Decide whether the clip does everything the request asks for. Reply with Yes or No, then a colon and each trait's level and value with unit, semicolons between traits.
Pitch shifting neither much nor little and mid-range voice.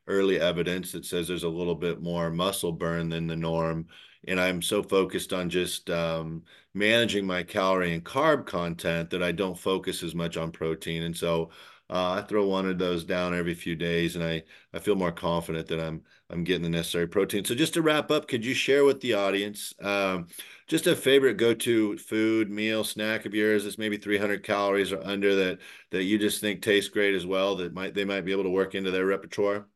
No: average, 3.3 semitones; very low, 95 Hz